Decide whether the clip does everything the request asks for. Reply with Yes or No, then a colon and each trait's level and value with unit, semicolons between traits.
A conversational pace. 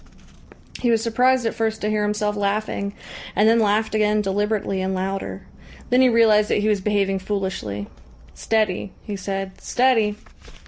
Yes: average, 155 wpm